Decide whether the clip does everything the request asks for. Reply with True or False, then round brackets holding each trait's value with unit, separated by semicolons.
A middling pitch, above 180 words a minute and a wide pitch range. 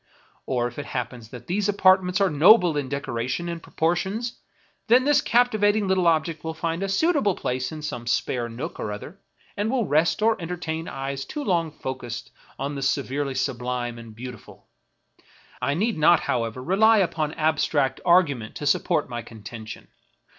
False (155 Hz; 170 wpm; 6.8 semitones)